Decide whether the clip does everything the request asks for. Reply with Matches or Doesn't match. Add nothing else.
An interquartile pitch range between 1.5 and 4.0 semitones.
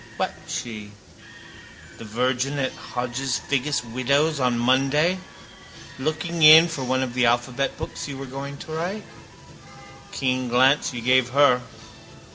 Matches